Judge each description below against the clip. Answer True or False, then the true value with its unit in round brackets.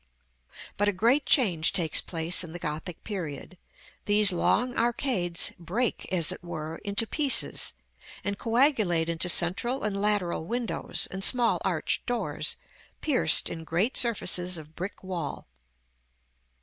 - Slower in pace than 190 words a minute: True (135 wpm)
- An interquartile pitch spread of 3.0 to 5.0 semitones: False (5.4 semitones)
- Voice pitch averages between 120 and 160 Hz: False (190 Hz)